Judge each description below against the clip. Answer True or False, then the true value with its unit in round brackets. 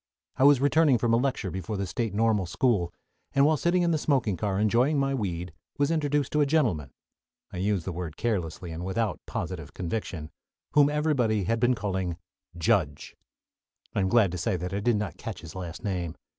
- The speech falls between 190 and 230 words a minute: True (200 wpm)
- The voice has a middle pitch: False (105 Hz)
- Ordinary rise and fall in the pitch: False (7.0 semitones)